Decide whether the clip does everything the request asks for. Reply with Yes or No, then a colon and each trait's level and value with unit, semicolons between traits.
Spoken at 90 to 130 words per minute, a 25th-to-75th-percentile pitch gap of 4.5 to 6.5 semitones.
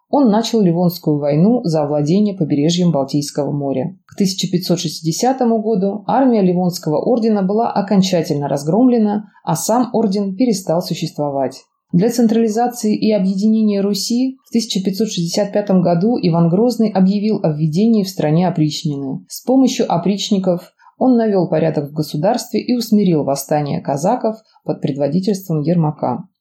Yes: average, 125 wpm; wide, 5.5 semitones